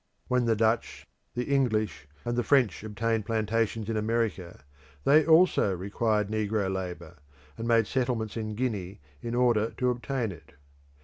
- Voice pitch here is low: Yes, low, 110 Hz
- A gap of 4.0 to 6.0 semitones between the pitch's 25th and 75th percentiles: No, average, 2.7 semitones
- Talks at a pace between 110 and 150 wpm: Yes, average, 145 wpm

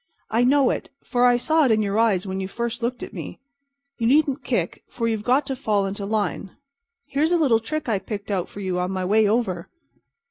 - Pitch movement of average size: Yes, average, 4.2 semitones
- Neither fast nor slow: No, fast, 225 wpm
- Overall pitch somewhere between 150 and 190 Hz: No, high, 225 Hz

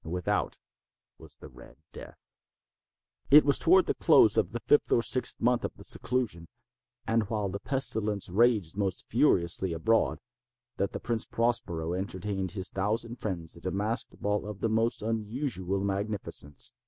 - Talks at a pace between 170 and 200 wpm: No, average, 155 wpm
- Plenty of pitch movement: No, average, 3.7 semitones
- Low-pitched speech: Yes, low, 105 Hz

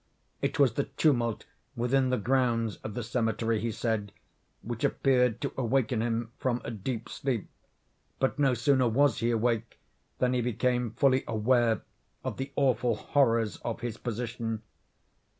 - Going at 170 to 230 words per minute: No, average, 150 wpm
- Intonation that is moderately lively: No, narrow, 2.2 semitones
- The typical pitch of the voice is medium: No, low, 120 Hz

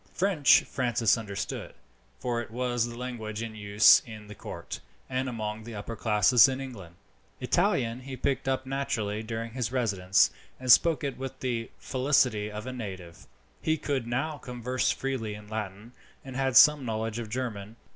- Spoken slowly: No, average, 165 wpm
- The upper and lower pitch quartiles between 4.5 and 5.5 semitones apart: No, average, 3.3 semitones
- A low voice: Yes, low, 120 Hz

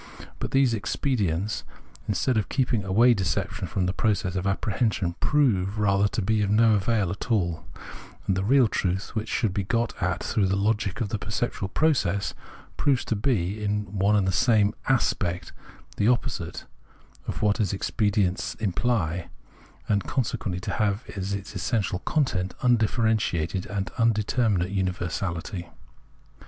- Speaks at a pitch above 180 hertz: No, low, 100 Hz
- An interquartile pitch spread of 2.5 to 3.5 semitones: Yes, average, 3.1 semitones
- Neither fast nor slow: Yes, average, 155 wpm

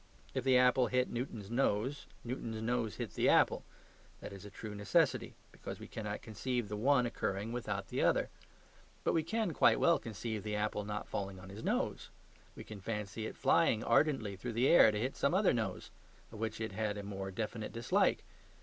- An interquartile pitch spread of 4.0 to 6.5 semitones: No, average, 3.3 semitones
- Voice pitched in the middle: No, low, 110 Hz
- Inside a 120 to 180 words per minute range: No, average, 195 wpm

